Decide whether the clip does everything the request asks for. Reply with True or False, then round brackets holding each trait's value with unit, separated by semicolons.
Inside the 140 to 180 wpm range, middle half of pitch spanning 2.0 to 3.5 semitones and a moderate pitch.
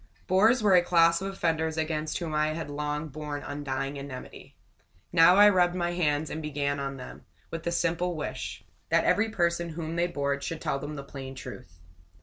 False (190 wpm; 3.2 semitones; 160 Hz)